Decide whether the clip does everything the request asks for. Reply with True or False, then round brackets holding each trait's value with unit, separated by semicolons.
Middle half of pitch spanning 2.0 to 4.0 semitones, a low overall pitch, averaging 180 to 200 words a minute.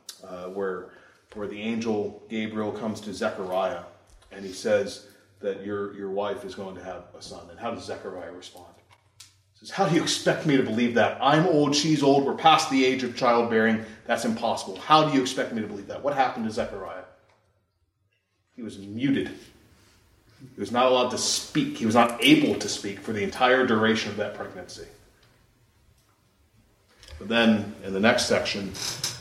True (3.7 semitones; 110 Hz; 185 wpm)